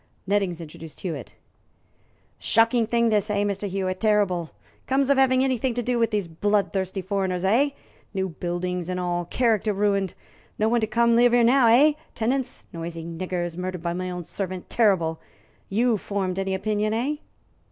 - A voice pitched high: Yes, high, 200 Hz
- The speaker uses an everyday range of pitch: Yes, average, 4.2 semitones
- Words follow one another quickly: No, average, 170 wpm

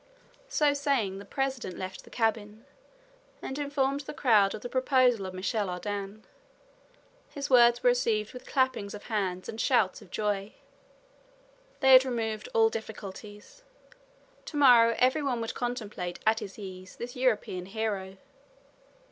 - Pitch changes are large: No, average, 4.1 semitones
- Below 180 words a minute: Yes, average, 145 wpm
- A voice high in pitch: Yes, high, 225 Hz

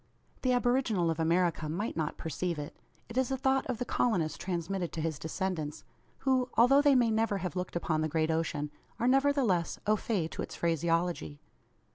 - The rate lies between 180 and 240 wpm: Yes, average, 185 wpm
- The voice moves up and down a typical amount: No, wide, 7.2 semitones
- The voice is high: No, medium, 180 Hz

